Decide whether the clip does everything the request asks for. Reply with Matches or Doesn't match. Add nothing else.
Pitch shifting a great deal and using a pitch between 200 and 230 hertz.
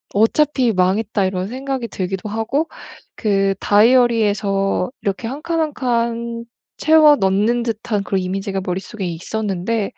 Doesn't match